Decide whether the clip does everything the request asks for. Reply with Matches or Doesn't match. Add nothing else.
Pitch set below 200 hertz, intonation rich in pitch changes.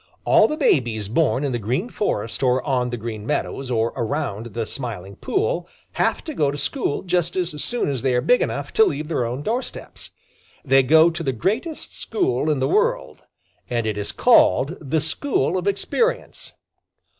Matches